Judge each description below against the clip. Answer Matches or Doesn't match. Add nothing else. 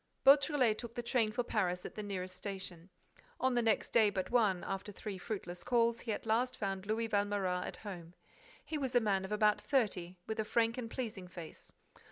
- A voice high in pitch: Matches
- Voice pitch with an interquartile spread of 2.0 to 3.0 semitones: Doesn't match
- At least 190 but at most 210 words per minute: Matches